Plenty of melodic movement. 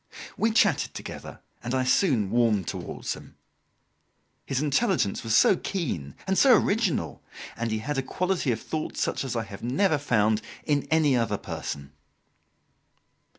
Yes: wide, 7.1 semitones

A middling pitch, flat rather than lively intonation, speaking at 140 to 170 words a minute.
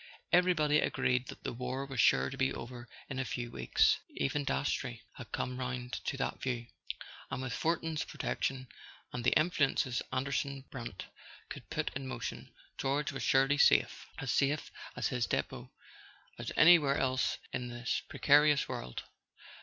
No: low, 130 Hz; narrow, 2.3 semitones; average, 155 wpm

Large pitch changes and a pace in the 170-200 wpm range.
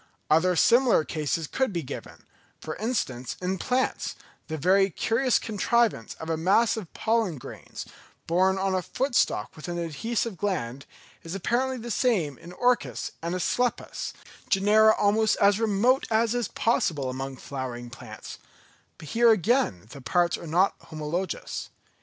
No: wide, 6.3 semitones; average, 150 wpm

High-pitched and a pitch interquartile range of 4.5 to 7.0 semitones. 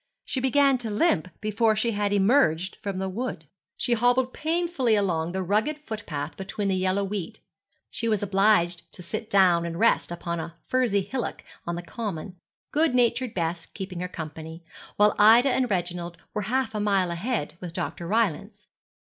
Yes: high, 205 Hz; average, 4.9 semitones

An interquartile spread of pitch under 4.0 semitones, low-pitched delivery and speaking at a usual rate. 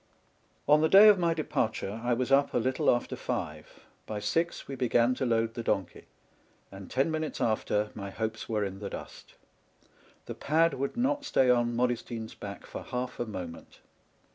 No: average, 4.6 semitones; low, 120 Hz; average, 180 wpm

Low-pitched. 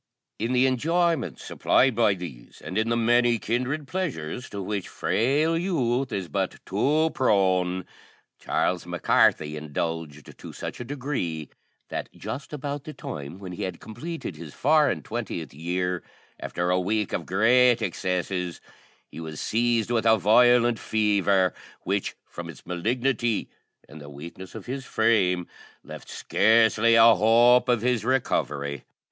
Yes: low, 110 Hz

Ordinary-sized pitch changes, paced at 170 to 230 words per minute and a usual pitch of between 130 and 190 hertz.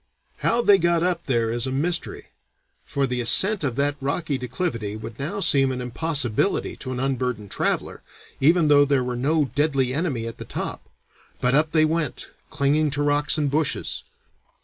Yes: average, 3.9 semitones; average, 175 wpm; medium, 140 Hz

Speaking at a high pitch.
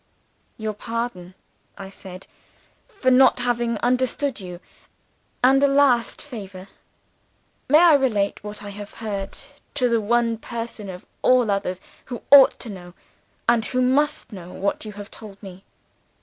Yes: high, 230 Hz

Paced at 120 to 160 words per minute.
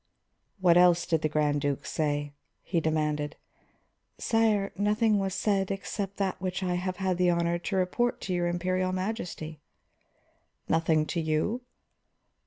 Yes: average, 145 wpm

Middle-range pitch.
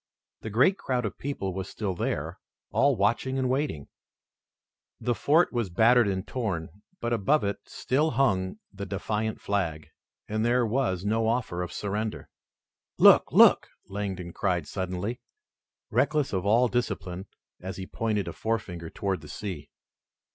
No: low, 105 Hz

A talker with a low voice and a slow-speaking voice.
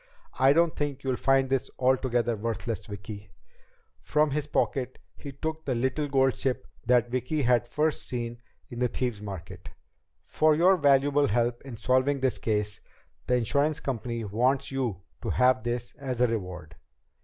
No: low, 125 Hz; average, 160 wpm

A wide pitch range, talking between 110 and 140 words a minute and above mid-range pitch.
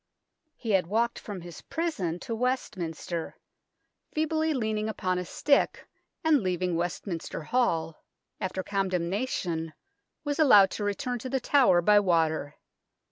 Yes: wide, 6.3 semitones; slow, 135 wpm; high, 200 Hz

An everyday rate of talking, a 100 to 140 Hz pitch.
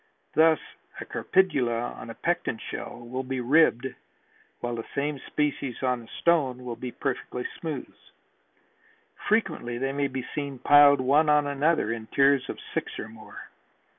Yes: average, 155 wpm; low, 135 Hz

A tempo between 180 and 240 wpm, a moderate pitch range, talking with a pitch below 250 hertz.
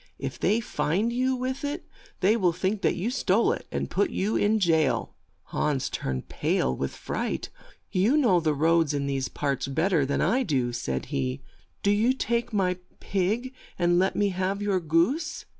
No: average, 190 wpm; wide, 7.1 semitones; medium, 185 Hz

